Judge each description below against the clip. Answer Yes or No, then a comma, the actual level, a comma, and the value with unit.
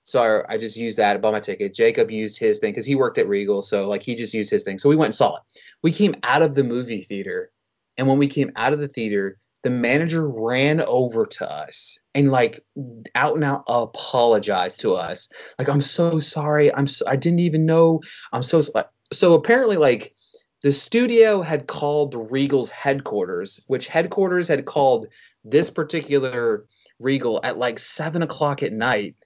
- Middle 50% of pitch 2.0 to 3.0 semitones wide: No, average, 4.9 semitones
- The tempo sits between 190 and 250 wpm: Yes, average, 195 wpm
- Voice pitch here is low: No, medium, 145 Hz